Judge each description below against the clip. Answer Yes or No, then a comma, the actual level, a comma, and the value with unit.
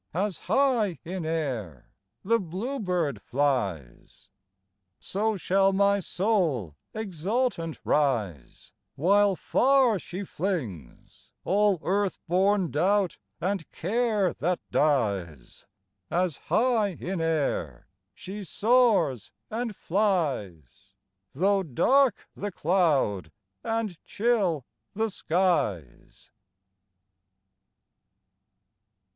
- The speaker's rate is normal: No, slow, 85 wpm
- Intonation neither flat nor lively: No, wide, 6.0 semitones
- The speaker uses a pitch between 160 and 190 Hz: Yes, medium, 185 Hz